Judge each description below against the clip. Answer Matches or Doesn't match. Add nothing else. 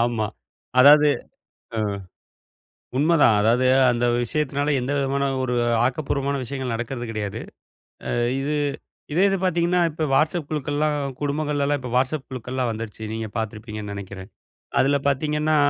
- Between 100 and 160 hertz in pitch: Matches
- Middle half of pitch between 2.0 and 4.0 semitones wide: Doesn't match